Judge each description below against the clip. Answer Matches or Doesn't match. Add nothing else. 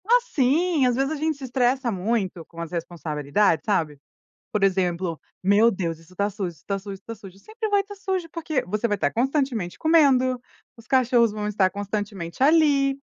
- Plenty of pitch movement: Matches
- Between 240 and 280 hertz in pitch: Doesn't match